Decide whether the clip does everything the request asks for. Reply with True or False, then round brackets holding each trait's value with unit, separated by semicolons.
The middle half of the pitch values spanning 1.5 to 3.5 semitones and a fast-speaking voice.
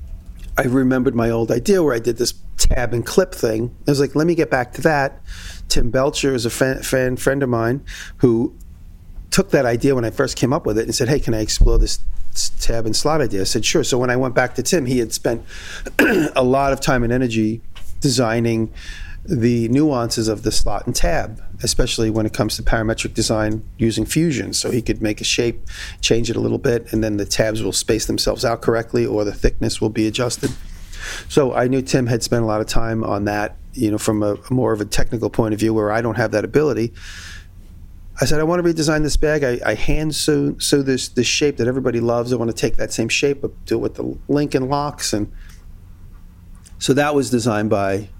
False (3.9 semitones; 230 wpm)